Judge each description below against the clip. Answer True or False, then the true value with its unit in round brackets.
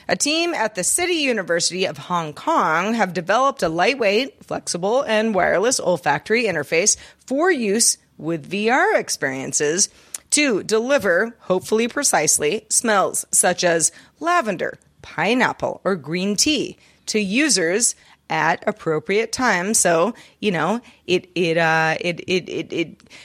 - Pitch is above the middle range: True (210 Hz)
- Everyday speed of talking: False (130 wpm)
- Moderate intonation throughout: False (5.9 semitones)